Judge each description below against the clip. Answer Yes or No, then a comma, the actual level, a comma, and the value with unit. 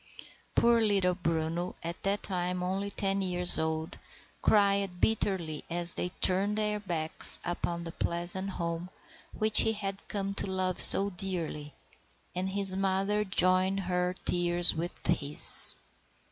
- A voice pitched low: No, medium, 185 Hz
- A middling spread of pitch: No, narrow, 2.3 semitones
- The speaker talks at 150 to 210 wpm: No, slow, 135 wpm